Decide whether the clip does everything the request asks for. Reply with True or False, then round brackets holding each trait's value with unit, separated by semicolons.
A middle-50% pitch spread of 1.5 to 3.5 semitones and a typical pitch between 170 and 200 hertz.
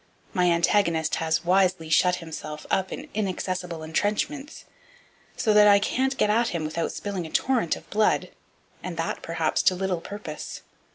False (3.9 semitones; 185 Hz)